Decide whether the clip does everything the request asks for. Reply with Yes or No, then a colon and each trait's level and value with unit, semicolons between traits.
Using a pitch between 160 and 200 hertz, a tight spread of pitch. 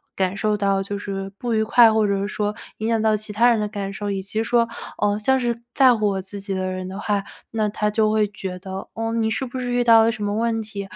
No: high, 210 Hz; narrow, 2.3 semitones